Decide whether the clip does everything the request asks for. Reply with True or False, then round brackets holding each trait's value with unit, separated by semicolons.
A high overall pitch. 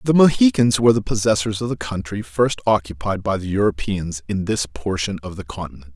False (100 Hz)